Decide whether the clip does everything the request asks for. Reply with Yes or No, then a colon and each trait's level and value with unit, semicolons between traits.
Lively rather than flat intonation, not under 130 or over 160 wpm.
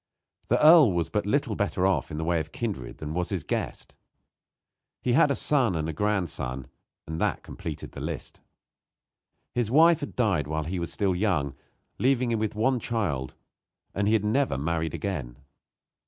No: wide, 6.6 semitones; average, 180 wpm